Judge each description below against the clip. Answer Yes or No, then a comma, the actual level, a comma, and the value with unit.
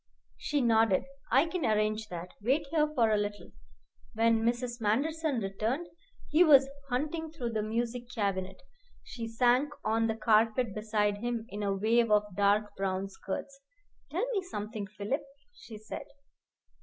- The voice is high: Yes, high, 225 Hz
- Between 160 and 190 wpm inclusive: No, average, 150 wpm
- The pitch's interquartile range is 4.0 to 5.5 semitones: No, average, 3.6 semitones